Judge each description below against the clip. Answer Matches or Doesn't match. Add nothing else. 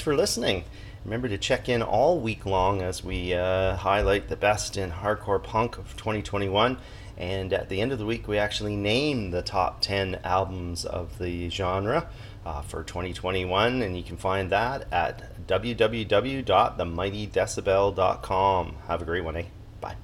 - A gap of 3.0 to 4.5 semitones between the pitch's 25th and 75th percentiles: Doesn't match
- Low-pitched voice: Matches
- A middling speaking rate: Matches